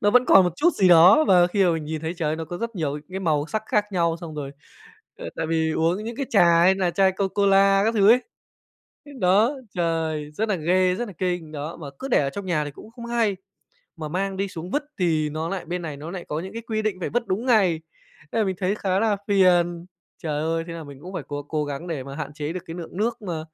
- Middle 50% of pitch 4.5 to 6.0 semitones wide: No, average, 3.9 semitones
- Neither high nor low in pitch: Yes, medium, 180 Hz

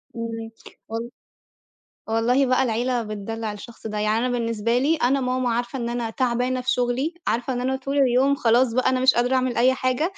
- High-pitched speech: Yes, high, 245 Hz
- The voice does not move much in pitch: Yes, narrow, 2.0 semitones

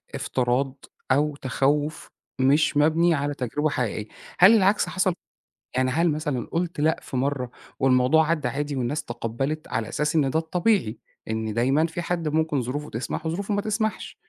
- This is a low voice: No, medium, 150 Hz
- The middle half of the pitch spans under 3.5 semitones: No, average, 3.9 semitones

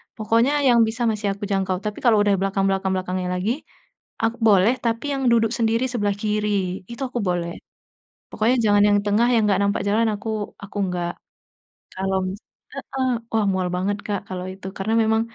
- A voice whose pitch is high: Yes, high, 205 Hz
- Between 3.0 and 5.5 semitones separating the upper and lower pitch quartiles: No, narrow, 2.6 semitones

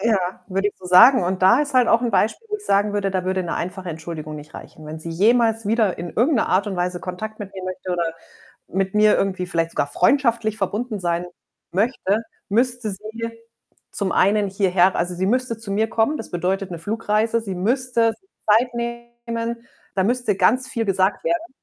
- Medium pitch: No, high, 205 Hz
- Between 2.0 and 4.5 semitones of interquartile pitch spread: Yes, average, 4.0 semitones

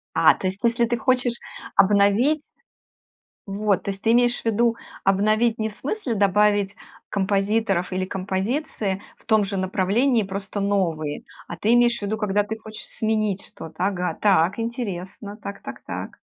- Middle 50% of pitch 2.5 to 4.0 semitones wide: Yes, average, 2.8 semitones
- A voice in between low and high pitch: No, high, 205 Hz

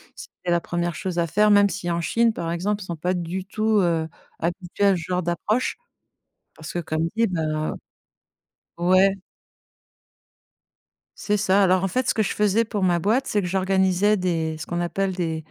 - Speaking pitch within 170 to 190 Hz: Yes, medium, 185 Hz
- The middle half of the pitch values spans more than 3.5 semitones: No, average, 2.9 semitones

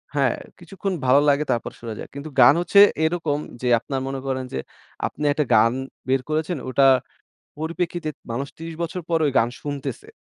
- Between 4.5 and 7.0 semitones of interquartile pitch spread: No, average, 3.8 semitones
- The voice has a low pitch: No, medium, 145 Hz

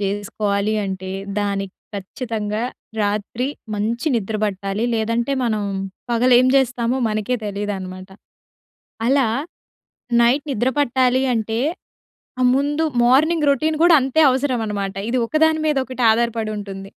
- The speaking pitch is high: Yes, high, 230 Hz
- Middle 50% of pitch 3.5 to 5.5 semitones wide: Yes, average, 4.0 semitones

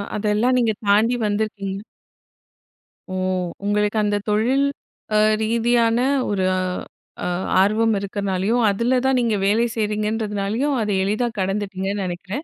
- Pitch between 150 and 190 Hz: No, high, 210 Hz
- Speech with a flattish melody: Yes, narrow, 2.3 semitones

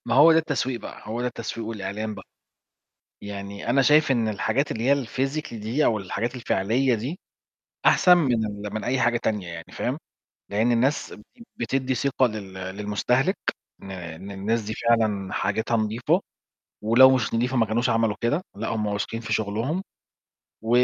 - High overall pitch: No, low, 115 Hz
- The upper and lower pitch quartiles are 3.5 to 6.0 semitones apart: Yes, average, 3.9 semitones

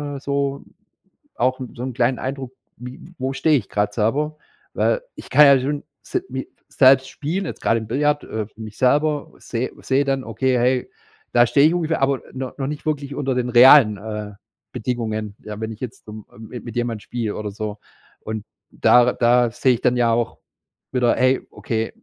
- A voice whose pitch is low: Yes, low, 125 Hz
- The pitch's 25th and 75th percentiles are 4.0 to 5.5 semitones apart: No, average, 3.3 semitones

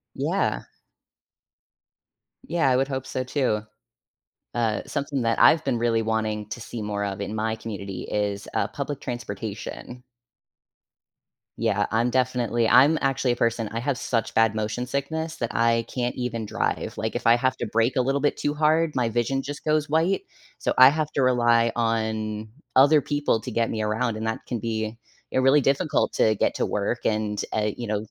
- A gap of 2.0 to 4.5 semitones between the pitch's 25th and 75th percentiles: Yes, average, 3.4 semitones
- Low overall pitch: Yes, low, 120 Hz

